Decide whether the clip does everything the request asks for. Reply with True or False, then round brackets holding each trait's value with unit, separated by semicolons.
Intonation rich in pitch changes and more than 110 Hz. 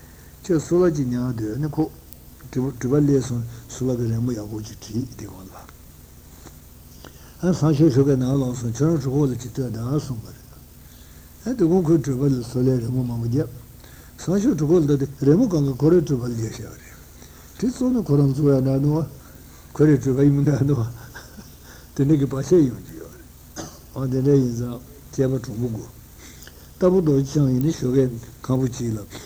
False (3.9 semitones; 130 Hz)